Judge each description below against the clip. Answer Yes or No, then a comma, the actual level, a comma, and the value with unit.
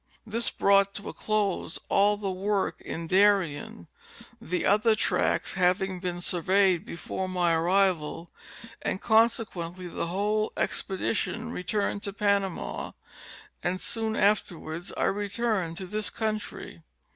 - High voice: Yes, high, 195 Hz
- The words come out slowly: Yes, slow, 125 wpm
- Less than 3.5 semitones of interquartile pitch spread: Yes, average, 2.8 semitones